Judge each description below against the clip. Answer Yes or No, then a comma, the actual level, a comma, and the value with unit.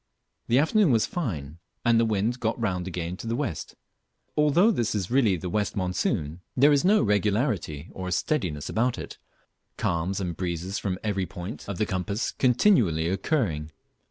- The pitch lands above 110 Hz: No, low, 100 Hz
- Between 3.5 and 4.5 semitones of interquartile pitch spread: No, average, 5.3 semitones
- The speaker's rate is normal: Yes, average, 170 wpm